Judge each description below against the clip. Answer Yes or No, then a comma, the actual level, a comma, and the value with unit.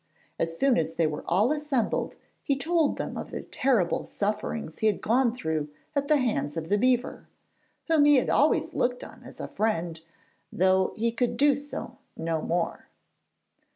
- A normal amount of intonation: No, wide, 8.3 semitones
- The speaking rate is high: No, average, 175 wpm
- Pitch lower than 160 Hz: No, high, 225 Hz